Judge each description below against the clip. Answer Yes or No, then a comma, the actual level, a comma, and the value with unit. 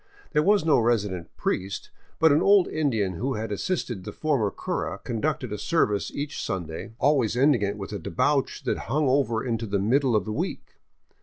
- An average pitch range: No, wide, 5.9 semitones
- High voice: No, low, 120 Hz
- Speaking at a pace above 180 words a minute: Yes, average, 190 wpm